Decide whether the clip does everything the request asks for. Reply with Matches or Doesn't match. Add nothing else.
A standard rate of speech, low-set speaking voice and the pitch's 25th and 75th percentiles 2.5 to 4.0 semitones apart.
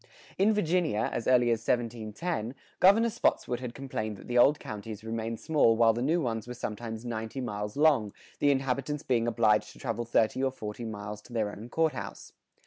Matches